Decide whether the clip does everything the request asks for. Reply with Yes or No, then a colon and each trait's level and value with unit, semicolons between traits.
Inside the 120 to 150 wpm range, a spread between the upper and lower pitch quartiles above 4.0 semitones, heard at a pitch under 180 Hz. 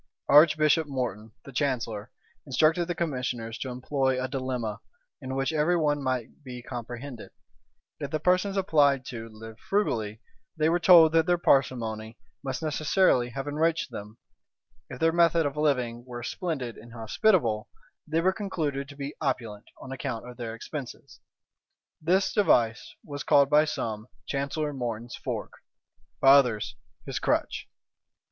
Yes: average, 145 wpm; average, 4.4 semitones; low, 135 Hz